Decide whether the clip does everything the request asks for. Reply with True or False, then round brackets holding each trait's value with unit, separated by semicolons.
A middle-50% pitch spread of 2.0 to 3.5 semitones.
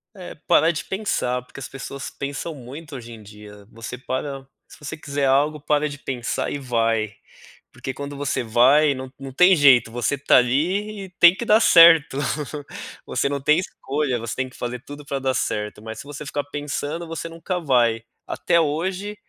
False (3.9 semitones)